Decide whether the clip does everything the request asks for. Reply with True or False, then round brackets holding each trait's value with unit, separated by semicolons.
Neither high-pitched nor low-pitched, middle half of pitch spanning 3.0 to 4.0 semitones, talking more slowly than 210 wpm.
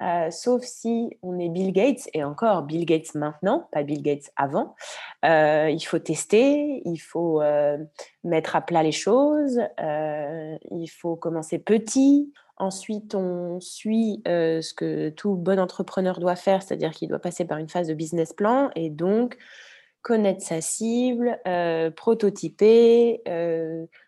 False (175 Hz; 5.3 semitones; 155 wpm)